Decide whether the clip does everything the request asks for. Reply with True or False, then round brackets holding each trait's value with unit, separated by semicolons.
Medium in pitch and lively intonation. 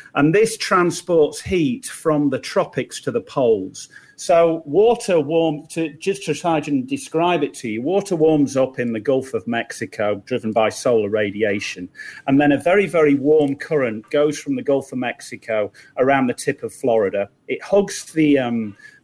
True (150 Hz; 6.0 semitones)